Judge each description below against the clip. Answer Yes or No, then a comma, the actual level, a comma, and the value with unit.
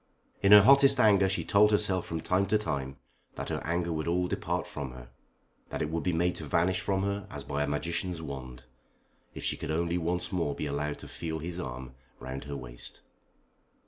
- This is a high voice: No, very low, 85 Hz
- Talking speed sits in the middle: No, fast, 210 wpm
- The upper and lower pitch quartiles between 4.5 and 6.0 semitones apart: Yes, average, 5.0 semitones